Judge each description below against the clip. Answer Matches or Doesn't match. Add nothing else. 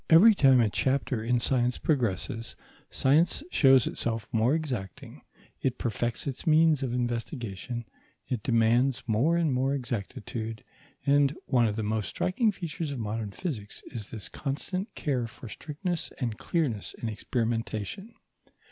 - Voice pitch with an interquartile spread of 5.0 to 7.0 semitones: Doesn't match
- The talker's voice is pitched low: Matches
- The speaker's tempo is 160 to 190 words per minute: Doesn't match